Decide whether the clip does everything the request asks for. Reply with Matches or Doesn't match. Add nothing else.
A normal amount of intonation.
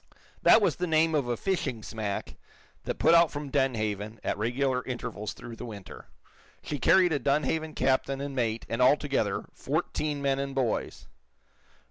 Matches